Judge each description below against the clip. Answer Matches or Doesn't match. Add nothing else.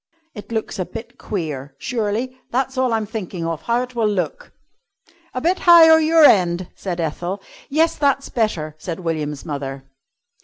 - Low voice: Doesn't match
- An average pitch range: Doesn't match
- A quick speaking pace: Doesn't match